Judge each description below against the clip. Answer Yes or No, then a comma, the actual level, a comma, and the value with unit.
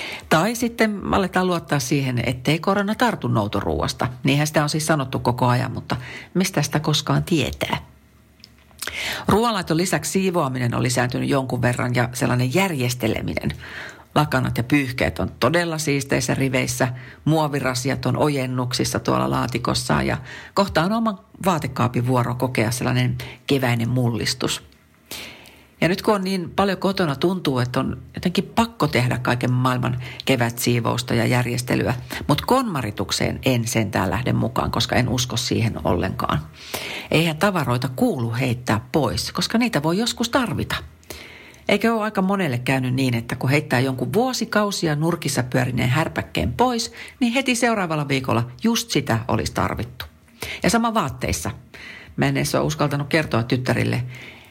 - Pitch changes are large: Yes, wide, 5.9 semitones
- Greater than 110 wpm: Yes, average, 140 wpm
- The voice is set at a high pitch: No, low, 135 Hz